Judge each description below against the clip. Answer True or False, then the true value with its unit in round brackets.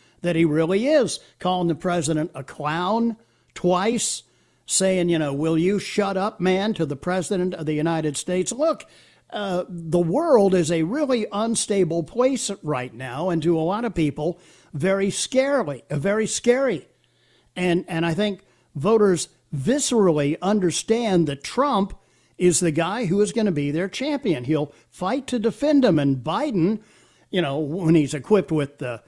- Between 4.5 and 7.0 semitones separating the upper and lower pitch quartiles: True (4.8 semitones)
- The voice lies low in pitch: False (180 Hz)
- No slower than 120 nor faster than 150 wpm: False (165 wpm)